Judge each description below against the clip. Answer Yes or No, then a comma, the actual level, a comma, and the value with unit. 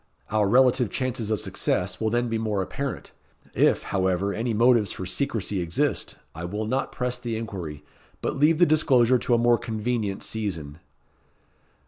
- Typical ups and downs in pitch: Yes, average, 4.0 semitones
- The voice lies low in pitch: Yes, low, 110 Hz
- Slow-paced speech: No, average, 160 wpm